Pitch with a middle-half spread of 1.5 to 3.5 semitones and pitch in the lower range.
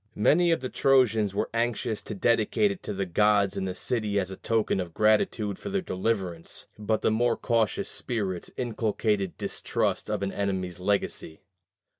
Yes: average, 3.2 semitones; low, 105 Hz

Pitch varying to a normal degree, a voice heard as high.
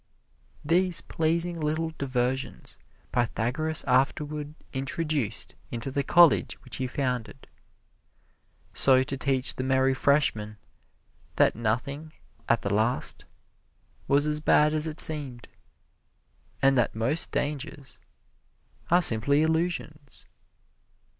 No: average, 3.5 semitones; medium, 140 Hz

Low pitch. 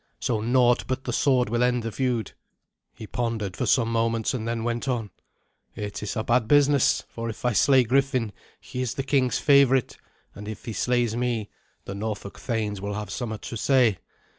Yes: low, 120 Hz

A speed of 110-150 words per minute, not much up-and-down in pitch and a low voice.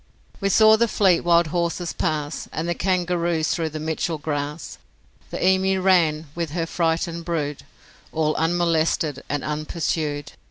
No: average, 145 wpm; narrow, 2.1 semitones; medium, 165 Hz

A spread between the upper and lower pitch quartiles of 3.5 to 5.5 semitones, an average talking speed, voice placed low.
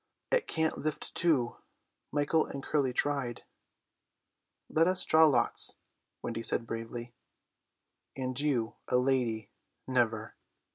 No: average, 4.2 semitones; slow, 110 wpm; low, 130 Hz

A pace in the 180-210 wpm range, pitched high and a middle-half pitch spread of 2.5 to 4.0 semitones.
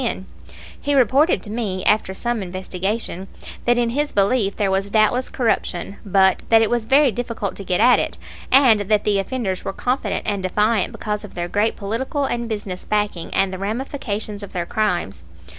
Yes: average, 185 wpm; high, 210 Hz; average, 3.6 semitones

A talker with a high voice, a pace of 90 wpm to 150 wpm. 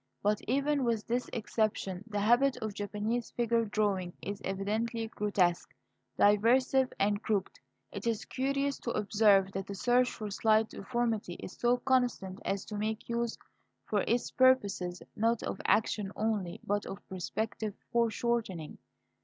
Yes: high, 215 Hz; average, 145 wpm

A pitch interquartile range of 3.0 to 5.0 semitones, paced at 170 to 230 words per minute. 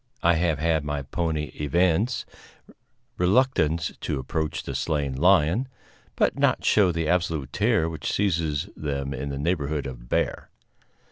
No: average, 3.3 semitones; average, 140 wpm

